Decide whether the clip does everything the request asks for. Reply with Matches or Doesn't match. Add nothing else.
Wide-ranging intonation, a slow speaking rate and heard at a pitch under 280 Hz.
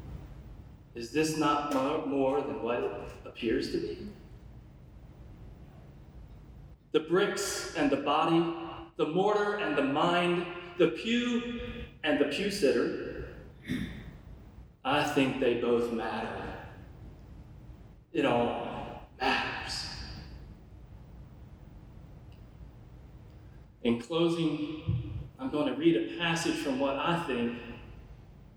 Matches